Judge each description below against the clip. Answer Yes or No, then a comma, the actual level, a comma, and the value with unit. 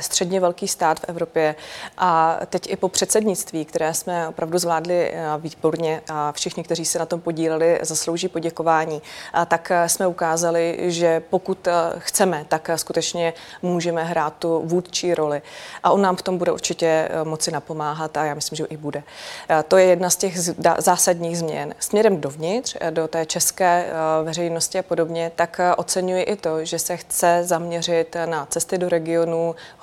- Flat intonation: Yes, narrow, 1.7 semitones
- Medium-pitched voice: Yes, medium, 170 Hz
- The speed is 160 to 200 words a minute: Yes, average, 165 wpm